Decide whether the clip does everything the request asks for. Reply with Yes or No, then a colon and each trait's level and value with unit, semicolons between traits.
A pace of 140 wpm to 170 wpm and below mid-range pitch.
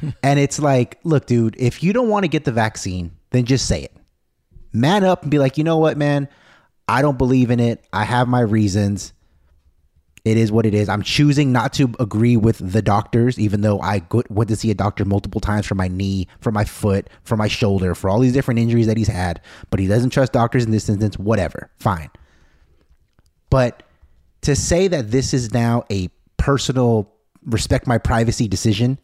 No: fast, 205 wpm; low, 110 Hz